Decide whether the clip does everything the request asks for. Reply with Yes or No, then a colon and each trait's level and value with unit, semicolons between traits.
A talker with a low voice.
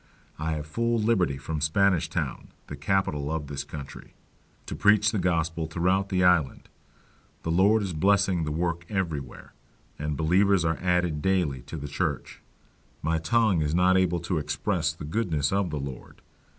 Yes: very low, 85 Hz